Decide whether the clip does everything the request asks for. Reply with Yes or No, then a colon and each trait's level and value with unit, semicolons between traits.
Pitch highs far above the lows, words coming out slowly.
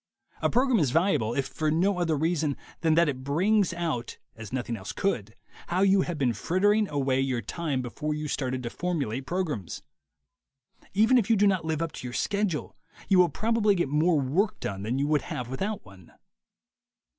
No: wide, 6.4 semitones; average, 195 wpm